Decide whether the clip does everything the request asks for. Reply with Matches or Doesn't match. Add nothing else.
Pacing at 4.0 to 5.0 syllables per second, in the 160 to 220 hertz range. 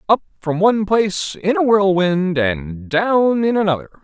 Matches